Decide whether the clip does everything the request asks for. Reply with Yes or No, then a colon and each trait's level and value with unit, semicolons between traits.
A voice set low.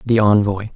Yes: low, 105 Hz